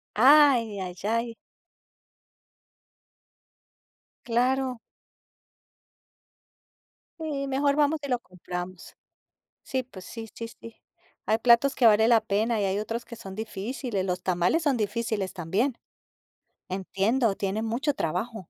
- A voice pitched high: Yes, high, 230 Hz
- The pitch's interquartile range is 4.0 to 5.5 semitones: Yes, average, 4.6 semitones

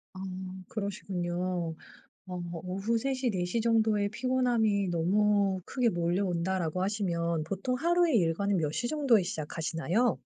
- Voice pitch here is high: Yes, high, 195 Hz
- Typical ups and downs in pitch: Yes, average, 4.3 semitones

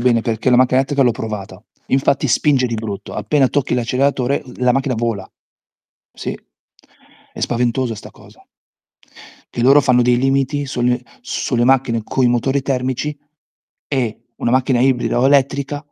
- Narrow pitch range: Yes, narrow, 2.2 semitones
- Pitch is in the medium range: No, low, 125 Hz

